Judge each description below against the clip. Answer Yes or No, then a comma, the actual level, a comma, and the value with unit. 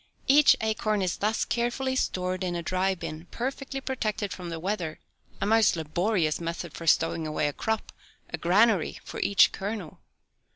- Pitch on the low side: No, high, 190 Hz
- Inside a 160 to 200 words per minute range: Yes, average, 165 wpm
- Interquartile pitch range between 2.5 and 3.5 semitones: No, average, 4.6 semitones